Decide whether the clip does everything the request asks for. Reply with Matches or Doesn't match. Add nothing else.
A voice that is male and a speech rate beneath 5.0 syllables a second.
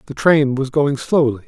Matches